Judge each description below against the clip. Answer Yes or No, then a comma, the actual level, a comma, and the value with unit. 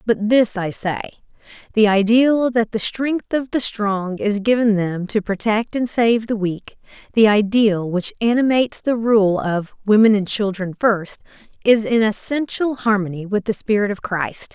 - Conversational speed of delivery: Yes, average, 170 wpm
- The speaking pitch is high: Yes, high, 215 Hz